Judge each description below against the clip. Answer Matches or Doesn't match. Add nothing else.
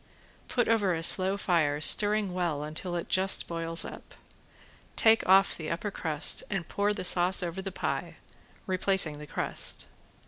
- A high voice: Doesn't match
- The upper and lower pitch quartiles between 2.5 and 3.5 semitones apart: Matches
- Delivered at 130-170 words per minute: Matches